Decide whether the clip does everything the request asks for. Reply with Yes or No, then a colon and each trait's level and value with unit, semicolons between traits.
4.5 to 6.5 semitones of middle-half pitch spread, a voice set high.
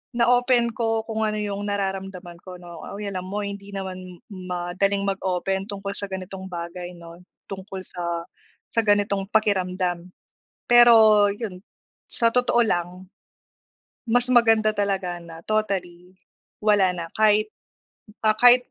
No: average, 2.9 semitones; high, 195 Hz